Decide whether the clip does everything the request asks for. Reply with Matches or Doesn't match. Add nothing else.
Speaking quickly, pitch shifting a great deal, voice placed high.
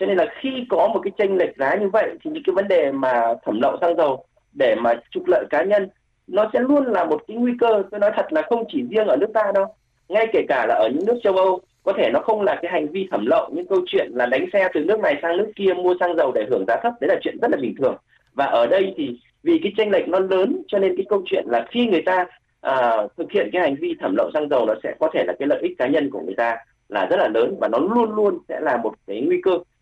Matches